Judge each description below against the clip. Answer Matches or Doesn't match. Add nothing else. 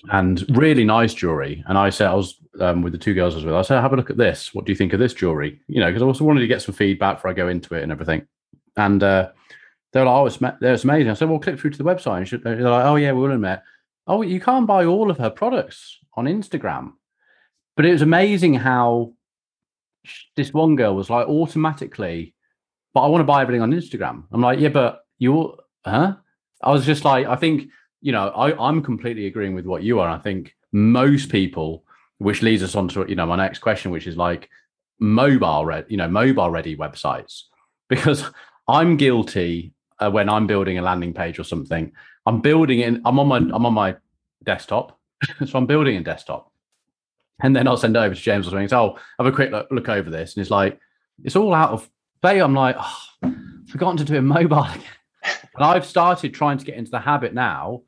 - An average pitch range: Doesn't match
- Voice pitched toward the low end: Matches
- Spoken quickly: Matches